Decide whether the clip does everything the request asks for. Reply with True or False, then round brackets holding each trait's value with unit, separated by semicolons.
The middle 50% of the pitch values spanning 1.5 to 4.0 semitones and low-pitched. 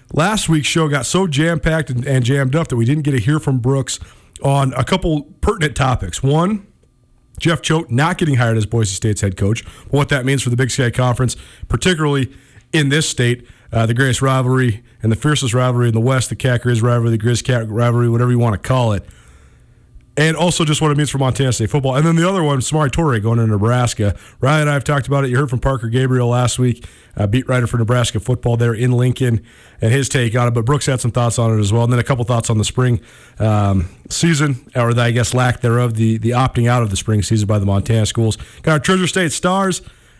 True (3.6 semitones; 125 Hz)